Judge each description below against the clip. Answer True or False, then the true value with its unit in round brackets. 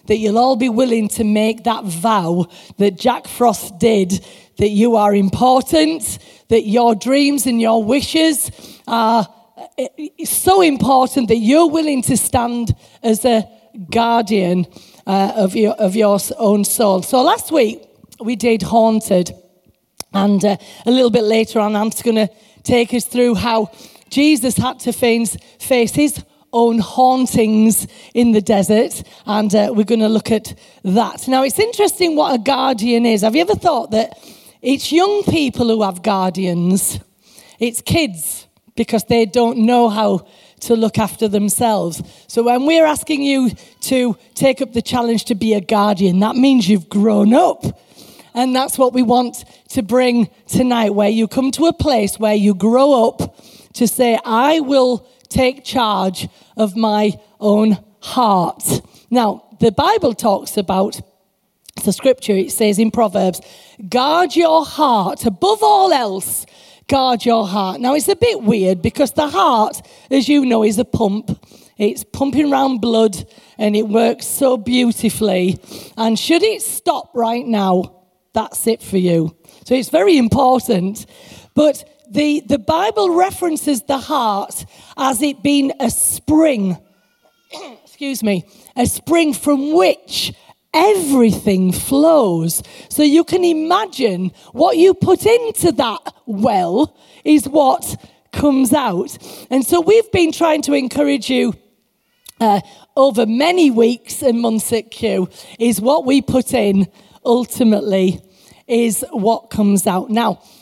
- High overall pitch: True (235 Hz)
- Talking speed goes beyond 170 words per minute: False (150 wpm)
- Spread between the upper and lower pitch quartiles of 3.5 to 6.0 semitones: True (4.4 semitones)